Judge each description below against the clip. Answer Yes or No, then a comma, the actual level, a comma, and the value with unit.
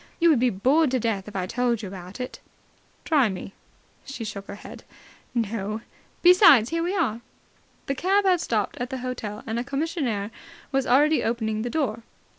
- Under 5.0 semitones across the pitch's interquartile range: No, wide, 5.4 semitones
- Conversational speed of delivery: Yes, average, 185 wpm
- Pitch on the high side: Yes, high, 245 Hz